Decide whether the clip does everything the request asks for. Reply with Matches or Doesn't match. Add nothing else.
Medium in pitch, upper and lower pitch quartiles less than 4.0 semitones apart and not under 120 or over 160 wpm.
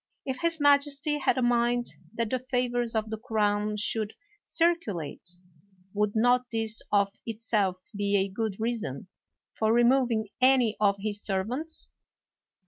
Doesn't match